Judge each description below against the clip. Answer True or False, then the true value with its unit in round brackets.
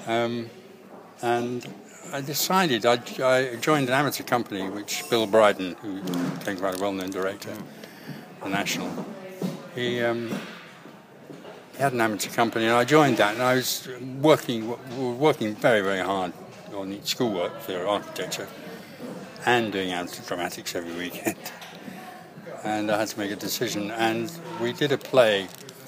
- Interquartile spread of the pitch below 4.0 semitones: False (5.0 semitones)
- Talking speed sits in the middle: True (150 wpm)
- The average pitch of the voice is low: True (120 Hz)